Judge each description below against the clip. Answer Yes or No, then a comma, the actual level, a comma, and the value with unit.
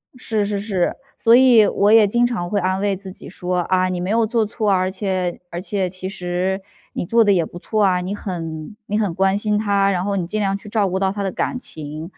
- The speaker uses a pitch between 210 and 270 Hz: No, high, 195 Hz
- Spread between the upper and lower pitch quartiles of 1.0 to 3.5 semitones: Yes, narrow, 2.4 semitones